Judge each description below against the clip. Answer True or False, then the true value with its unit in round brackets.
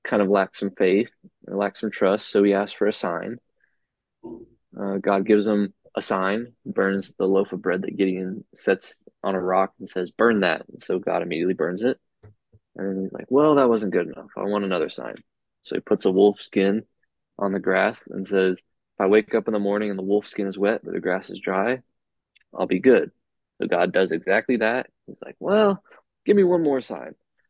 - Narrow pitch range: True (1.7 semitones)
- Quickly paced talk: True (215 wpm)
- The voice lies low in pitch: True (100 Hz)